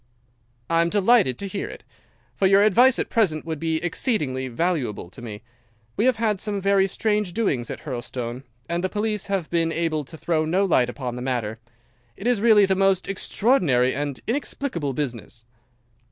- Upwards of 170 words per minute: Yes, average, 180 wpm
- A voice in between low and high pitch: Yes, medium, 170 Hz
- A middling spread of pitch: No, wide, 7.6 semitones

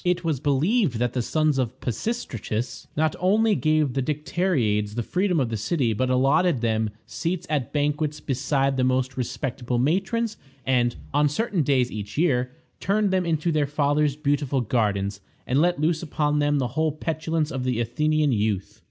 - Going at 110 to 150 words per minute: No, average, 180 wpm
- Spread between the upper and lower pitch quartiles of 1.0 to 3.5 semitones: No, average, 4.3 semitones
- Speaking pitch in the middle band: Yes, medium, 145 Hz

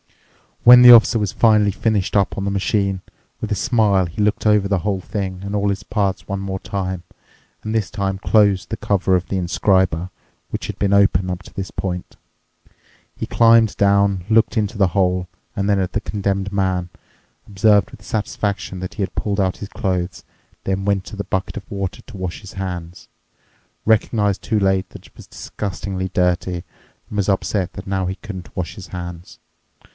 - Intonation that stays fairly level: Yes, narrow, 1.8 semitones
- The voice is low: Yes, low, 100 Hz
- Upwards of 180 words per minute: Yes, average, 190 wpm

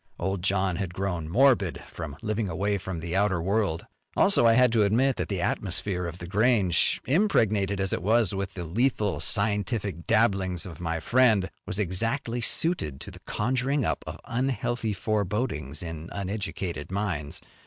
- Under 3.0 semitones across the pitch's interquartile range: No, average, 4.3 semitones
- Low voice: Yes, low, 100 Hz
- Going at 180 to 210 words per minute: No, average, 165 wpm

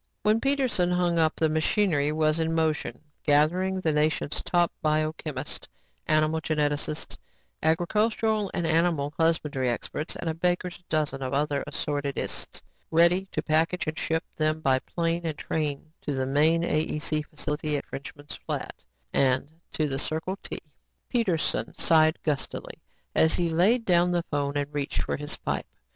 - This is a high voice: No, medium, 155 Hz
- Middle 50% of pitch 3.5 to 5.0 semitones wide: No, average, 2.7 semitones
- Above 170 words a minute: No, average, 155 wpm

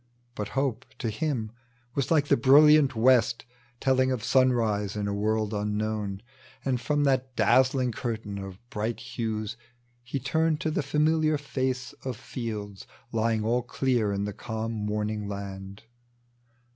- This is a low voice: Yes, low, 115 Hz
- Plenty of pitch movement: No, average, 3.9 semitones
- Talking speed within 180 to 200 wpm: No, average, 145 wpm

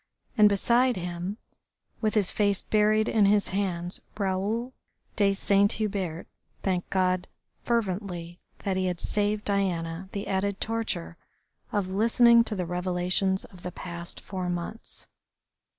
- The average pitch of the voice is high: Yes, high, 195 Hz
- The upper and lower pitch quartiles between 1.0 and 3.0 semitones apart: Yes, average, 2.7 semitones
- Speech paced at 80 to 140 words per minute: Yes, slow, 135 wpm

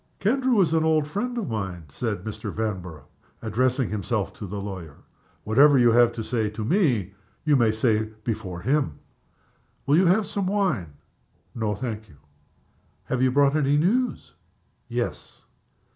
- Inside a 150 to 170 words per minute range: Yes, average, 155 wpm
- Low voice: Yes, low, 120 Hz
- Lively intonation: Yes, wide, 6.5 semitones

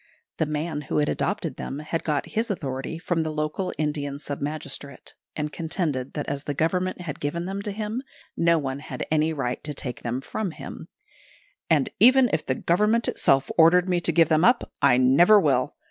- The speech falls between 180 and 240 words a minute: Yes, average, 195 wpm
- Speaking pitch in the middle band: Yes, medium, 155 Hz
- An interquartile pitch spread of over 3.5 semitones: Yes, average, 4.0 semitones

